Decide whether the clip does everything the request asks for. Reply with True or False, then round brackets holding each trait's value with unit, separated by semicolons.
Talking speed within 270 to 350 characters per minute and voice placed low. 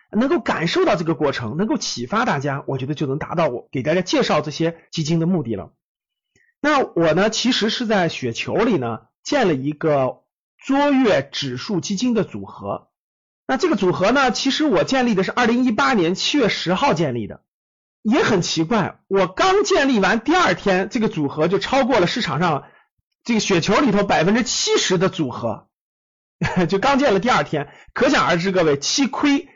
False (280 characters per minute; 195 Hz)